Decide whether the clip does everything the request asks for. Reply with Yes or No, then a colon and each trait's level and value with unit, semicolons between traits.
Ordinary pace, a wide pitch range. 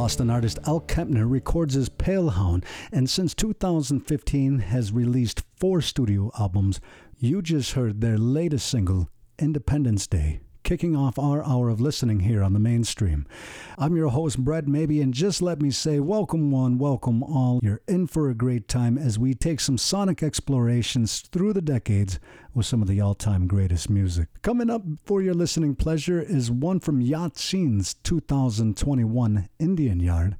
Yes: average, 165 wpm; wide, 6.2 semitones